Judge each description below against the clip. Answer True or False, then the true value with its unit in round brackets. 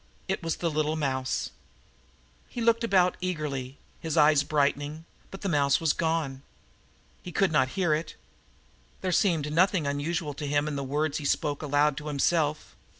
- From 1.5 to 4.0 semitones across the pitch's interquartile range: True (2.7 semitones)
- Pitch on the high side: False (155 Hz)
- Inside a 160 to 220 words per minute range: True (165 wpm)